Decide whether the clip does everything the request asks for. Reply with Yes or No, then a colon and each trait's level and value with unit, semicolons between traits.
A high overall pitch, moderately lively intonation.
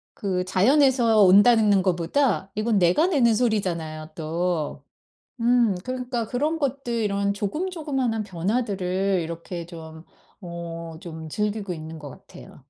No: high, 200 Hz; wide, 5.8 semitones